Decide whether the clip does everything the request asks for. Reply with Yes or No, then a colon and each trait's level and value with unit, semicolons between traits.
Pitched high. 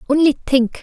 Yes: very high, 280 Hz